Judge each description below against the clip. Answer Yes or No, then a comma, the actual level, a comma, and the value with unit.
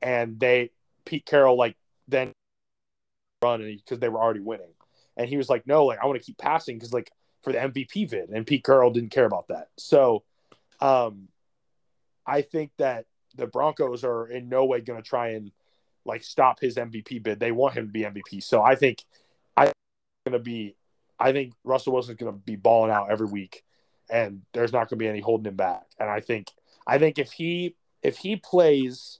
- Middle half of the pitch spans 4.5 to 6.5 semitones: No, average, 3.2 semitones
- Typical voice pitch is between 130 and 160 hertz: No, low, 120 Hz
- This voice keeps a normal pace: No, fast, 210 wpm